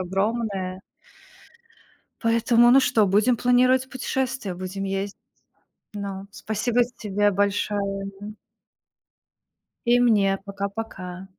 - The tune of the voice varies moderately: Yes, average, 3.4 semitones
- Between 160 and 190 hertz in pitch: No, high, 205 Hz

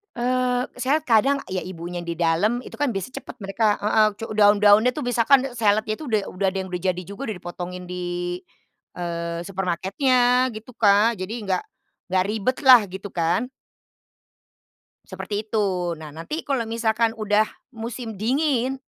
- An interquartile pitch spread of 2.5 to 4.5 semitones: No, average, 5.2 semitones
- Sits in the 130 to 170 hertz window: No, high, 215 Hz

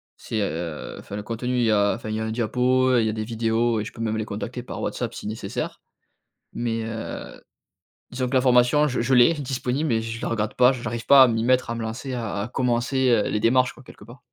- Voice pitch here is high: No, low, 120 Hz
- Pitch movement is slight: Yes, narrow, 2.3 semitones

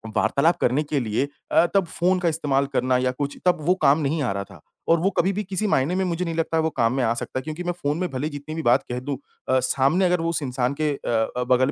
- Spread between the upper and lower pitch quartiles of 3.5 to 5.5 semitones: Yes, average, 4.8 semitones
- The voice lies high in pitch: No, medium, 145 Hz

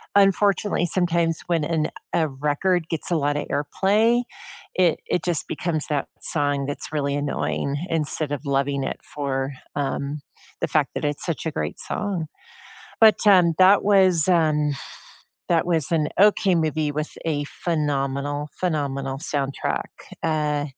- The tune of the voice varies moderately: Yes, average, 3.4 semitones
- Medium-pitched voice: Yes, medium, 155 Hz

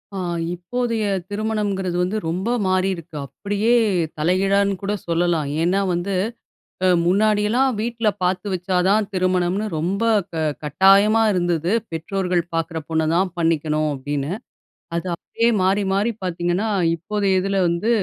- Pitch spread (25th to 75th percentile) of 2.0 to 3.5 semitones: Yes, average, 3.2 semitones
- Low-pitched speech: No, medium, 185 Hz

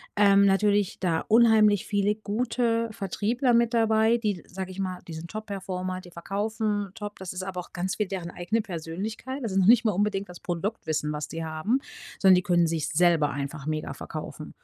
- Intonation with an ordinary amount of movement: Yes, average, 3.6 semitones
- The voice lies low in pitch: No, high, 195 Hz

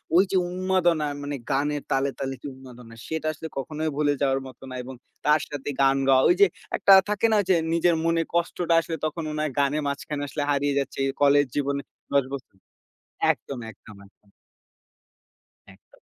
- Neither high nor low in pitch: Yes, medium, 145 Hz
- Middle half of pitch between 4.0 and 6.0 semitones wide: No, average, 3.0 semitones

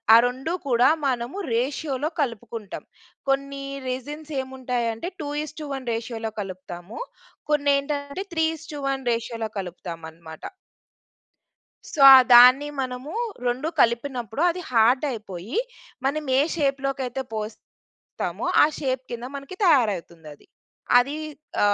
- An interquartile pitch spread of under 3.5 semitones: No, average, 3.8 semitones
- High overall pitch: Yes, very high, 255 Hz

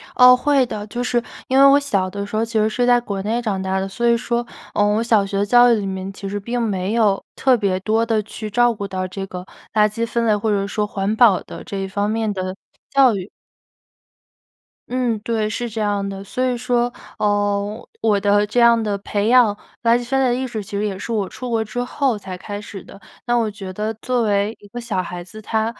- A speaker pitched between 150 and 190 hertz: No, high, 215 Hz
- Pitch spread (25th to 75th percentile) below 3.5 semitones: Yes, average, 3.0 semitones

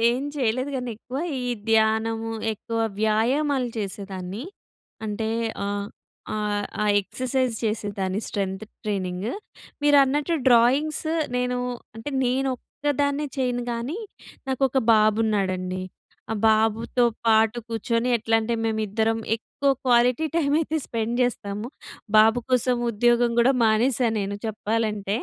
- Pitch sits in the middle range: No, high, 225 Hz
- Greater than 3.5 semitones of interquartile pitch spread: No, average, 2.9 semitones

